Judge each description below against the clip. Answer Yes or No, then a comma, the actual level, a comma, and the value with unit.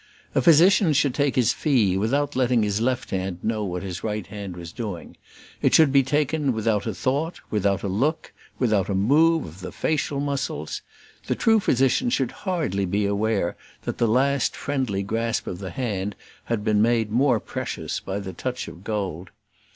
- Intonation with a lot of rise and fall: Yes, wide, 5.8 semitones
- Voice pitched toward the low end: Yes, low, 115 Hz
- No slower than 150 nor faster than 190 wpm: Yes, average, 180 wpm